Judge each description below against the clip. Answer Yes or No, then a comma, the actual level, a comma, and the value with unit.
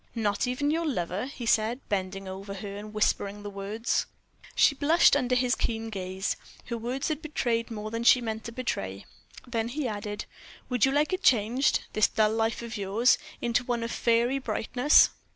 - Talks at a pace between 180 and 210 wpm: Yes, average, 185 wpm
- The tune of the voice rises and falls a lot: No, average, 3.4 semitones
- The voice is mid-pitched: No, high, 230 Hz